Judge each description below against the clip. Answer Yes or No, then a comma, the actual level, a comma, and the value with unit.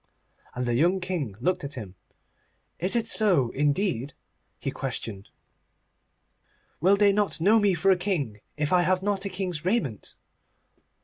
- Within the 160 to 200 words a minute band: No, average, 150 wpm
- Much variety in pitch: Yes, wide, 5.8 semitones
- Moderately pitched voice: Yes, medium, 180 Hz